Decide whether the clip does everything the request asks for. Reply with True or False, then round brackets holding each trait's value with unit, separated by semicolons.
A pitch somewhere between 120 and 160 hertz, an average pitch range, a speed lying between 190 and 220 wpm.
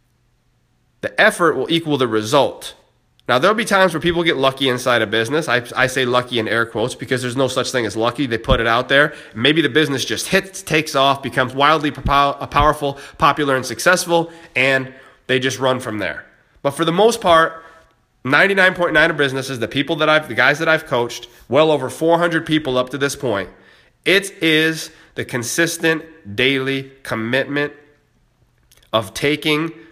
False (140 Hz; 4.3 semitones; 180 wpm)